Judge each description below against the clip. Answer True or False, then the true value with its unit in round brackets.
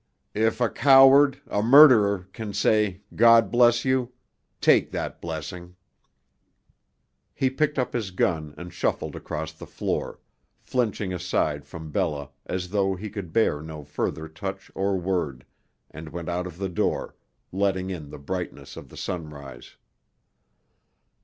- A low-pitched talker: True (95 Hz)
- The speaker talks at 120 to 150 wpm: True (140 wpm)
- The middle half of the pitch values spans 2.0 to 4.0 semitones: False (5.6 semitones)